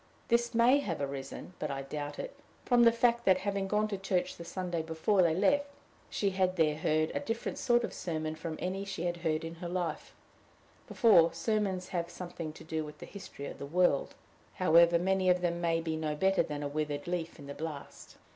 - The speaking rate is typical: No, fast, 210 wpm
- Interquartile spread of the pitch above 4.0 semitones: No, average, 3.5 semitones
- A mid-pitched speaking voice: Yes, medium, 175 Hz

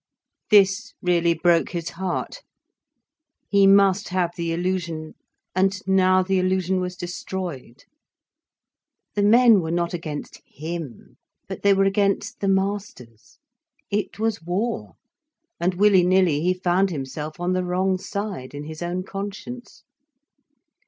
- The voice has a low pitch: No, medium, 185 Hz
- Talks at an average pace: No, slow, 130 wpm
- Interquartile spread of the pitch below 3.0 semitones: Yes, narrow, 2.4 semitones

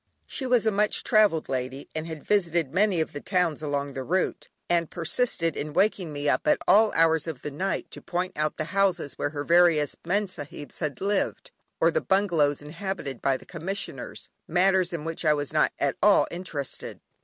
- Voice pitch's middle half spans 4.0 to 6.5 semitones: Yes, average, 4.4 semitones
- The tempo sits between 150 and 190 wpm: No, average, 200 wpm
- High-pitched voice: No, medium, 165 Hz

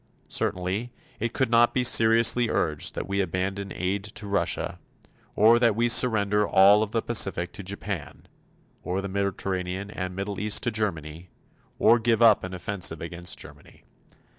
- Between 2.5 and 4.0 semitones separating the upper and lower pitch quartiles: Yes, average, 3.4 semitones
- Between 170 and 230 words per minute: No, average, 160 wpm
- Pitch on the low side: Yes, low, 100 Hz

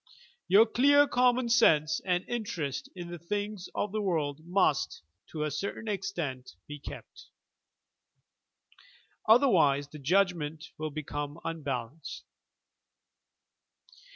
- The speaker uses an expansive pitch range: Yes, wide, 5.8 semitones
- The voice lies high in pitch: No, medium, 170 Hz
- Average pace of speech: No, slow, 110 wpm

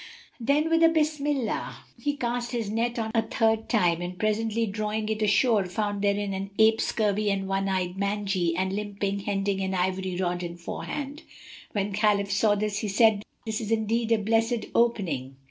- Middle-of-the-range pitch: No, high, 210 Hz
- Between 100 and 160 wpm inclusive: No, average, 175 wpm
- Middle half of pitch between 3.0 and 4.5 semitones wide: No, narrow, 2.6 semitones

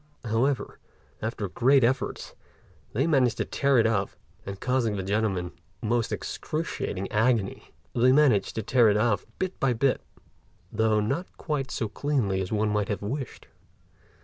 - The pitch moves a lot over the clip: No, average, 4.1 semitones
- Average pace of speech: No, slow, 125 wpm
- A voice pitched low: Yes, low, 115 Hz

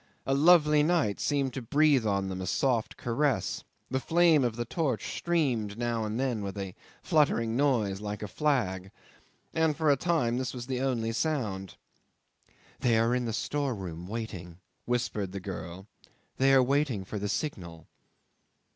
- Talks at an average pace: Yes, average, 165 wpm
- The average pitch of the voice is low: Yes, low, 120 Hz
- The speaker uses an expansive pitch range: Yes, wide, 5.7 semitones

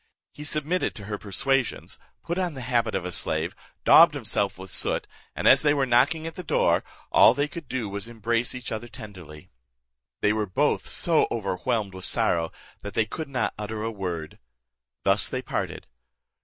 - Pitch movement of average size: No, wide, 6.0 semitones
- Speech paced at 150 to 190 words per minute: Yes, average, 185 wpm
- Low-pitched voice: Yes, low, 115 Hz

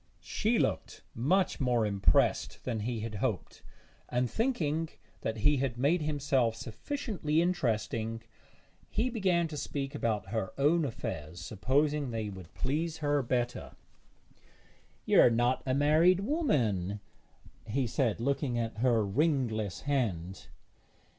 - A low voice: Yes, low, 130 Hz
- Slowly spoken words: Yes, slow, 125 wpm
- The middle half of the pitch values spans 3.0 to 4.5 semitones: No, wide, 5.4 semitones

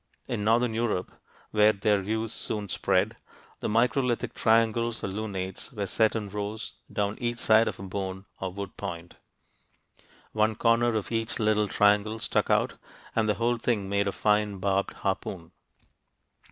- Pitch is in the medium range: No, low, 105 Hz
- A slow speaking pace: No, average, 155 wpm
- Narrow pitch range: Yes, narrow, 2.3 semitones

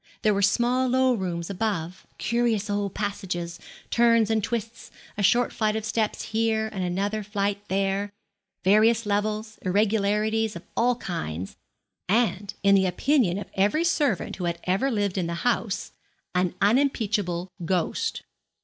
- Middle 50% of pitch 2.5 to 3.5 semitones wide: Yes, average, 2.8 semitones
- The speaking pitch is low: No, high, 205 Hz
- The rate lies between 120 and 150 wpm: Yes, average, 145 wpm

